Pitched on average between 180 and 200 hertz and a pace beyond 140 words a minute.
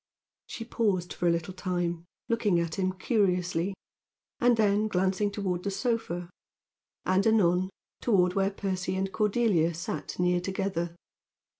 No: medium, 185 Hz; slow, 135 wpm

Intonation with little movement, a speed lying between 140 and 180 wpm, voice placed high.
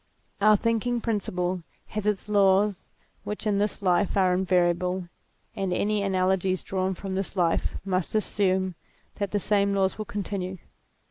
Yes: narrow, 2.0 semitones; average, 145 wpm; high, 195 Hz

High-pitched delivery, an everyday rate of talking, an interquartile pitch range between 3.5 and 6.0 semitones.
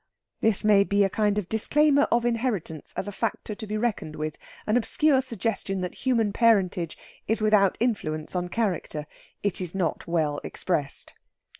Yes: high, 205 Hz; average, 165 wpm; average, 4.3 semitones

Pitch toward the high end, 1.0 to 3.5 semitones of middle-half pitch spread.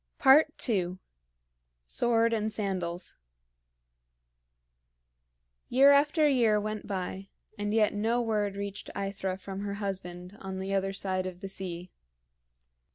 Yes: high, 200 Hz; average, 2.8 semitones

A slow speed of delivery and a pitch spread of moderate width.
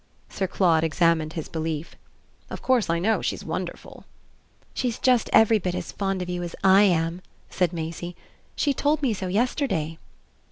No: average, 165 wpm; average, 5.0 semitones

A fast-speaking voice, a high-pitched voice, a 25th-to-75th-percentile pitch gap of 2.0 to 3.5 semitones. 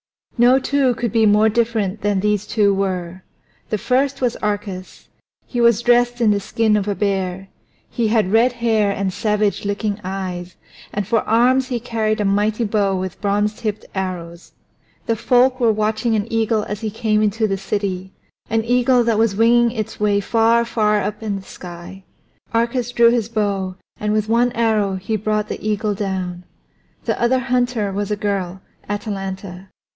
No: average, 175 wpm; high, 210 Hz; average, 2.8 semitones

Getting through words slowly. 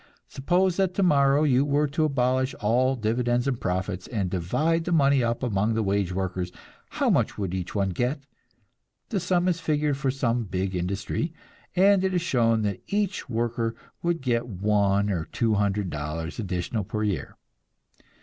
No: average, 170 wpm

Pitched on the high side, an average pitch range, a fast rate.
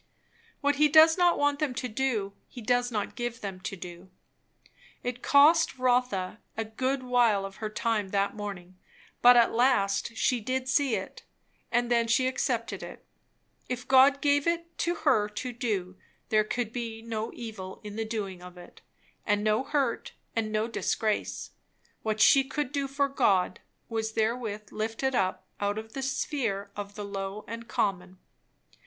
No: high, 230 Hz; average, 4.0 semitones; average, 170 wpm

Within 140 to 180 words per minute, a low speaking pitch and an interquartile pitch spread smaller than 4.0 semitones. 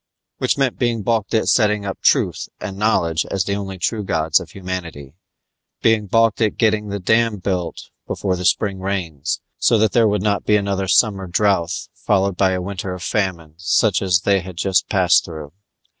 No: average, 190 wpm; very low, 95 Hz; average, 2.8 semitones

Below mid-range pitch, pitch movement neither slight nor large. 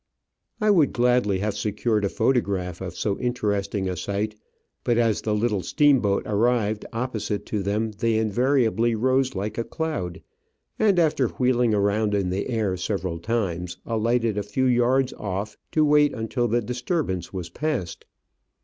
Yes: low, 110 Hz; average, 3.6 semitones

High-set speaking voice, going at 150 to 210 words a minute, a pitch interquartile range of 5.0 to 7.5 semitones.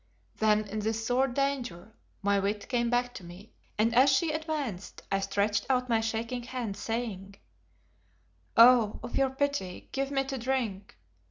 No: high, 230 Hz; average, 160 wpm; average, 4.3 semitones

